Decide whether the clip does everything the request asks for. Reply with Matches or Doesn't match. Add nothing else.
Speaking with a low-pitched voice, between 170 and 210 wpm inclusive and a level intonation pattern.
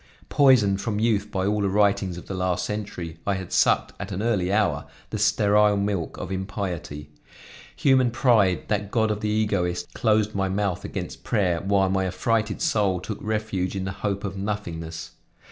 Matches